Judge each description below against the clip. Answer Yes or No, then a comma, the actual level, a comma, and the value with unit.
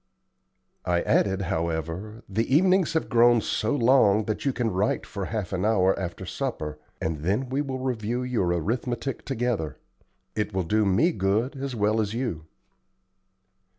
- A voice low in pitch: Yes, low, 110 Hz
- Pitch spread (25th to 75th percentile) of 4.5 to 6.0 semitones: Yes, average, 5.0 semitones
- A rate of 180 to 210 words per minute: No, average, 155 wpm